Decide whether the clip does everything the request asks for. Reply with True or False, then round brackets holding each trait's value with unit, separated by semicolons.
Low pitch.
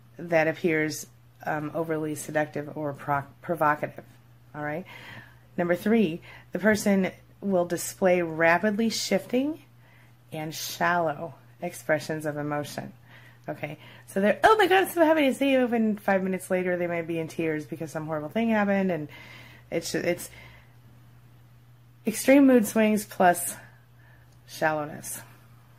False (155 Hz)